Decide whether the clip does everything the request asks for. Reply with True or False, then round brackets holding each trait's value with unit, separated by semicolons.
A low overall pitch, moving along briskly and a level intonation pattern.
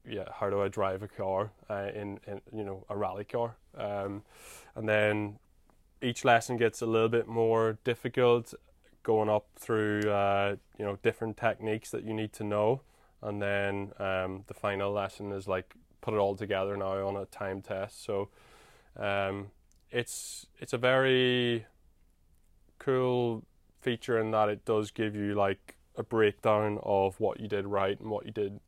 False (105 Hz; 170 wpm; 2.2 semitones)